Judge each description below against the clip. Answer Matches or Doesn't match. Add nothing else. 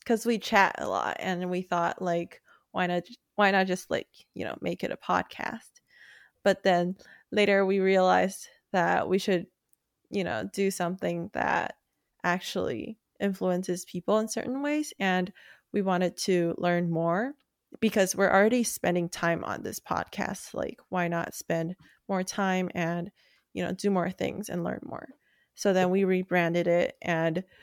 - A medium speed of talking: Matches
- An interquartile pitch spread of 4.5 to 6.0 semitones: Doesn't match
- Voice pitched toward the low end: Doesn't match